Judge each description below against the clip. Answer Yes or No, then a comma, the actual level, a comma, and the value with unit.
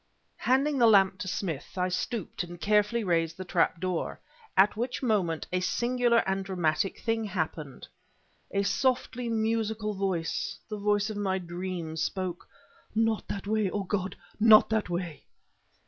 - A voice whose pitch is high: Yes, high, 200 Hz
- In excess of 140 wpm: Yes, average, 150 wpm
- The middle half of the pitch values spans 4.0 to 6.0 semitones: No, average, 3.5 semitones